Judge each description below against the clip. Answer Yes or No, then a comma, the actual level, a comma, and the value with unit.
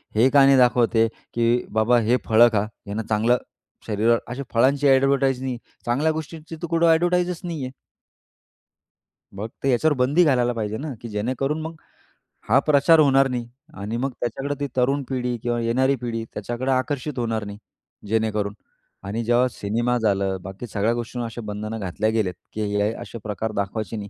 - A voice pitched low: Yes, low, 120 Hz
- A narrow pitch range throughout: No, average, 3.7 semitones